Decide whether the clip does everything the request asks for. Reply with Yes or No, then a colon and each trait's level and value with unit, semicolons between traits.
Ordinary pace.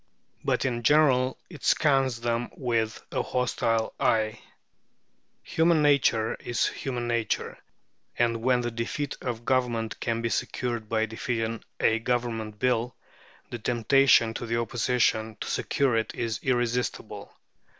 No: slow, 130 wpm